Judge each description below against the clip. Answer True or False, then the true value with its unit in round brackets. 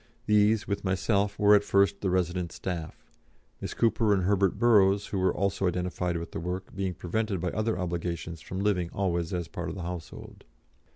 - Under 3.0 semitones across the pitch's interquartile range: True (2.5 semitones)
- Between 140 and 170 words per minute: False (185 wpm)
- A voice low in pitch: True (95 Hz)